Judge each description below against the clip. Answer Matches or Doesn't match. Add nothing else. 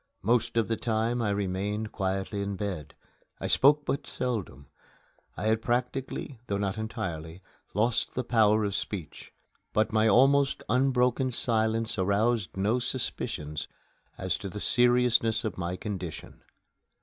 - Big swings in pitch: Doesn't match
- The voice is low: Matches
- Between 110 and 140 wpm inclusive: Matches